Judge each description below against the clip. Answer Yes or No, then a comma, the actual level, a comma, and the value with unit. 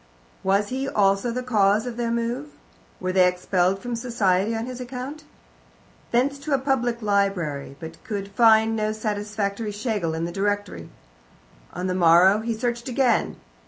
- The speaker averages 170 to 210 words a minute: No, average, 160 wpm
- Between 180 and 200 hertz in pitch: No, high, 215 Hz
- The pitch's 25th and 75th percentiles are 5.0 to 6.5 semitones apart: No, average, 3.7 semitones